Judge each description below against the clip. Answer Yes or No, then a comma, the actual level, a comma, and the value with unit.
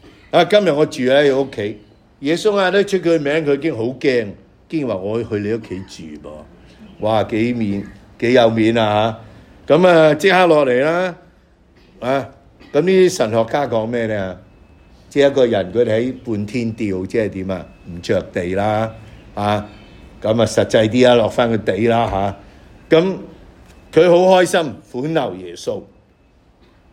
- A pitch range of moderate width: No, wide, 6.4 semitones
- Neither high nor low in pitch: No, low, 115 Hz